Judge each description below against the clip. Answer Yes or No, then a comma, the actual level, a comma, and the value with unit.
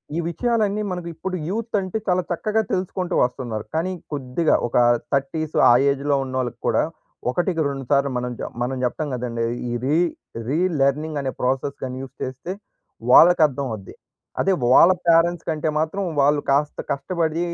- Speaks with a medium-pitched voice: Yes, medium, 150 Hz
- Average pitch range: Yes, average, 4.9 semitones